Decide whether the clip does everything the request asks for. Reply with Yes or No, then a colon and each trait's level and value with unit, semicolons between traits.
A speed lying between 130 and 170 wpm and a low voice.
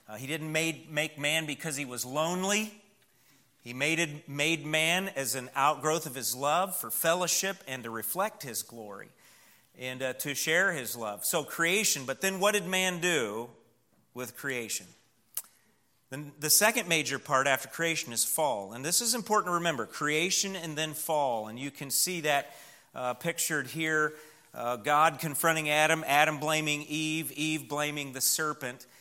No: average, 165 wpm; medium, 150 Hz